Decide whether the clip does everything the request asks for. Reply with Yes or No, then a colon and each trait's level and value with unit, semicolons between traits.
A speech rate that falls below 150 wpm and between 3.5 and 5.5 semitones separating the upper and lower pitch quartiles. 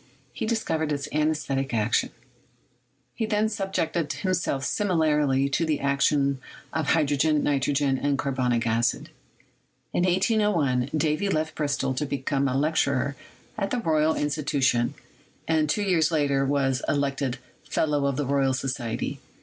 No: slow, 135 wpm; average, 2.8 semitones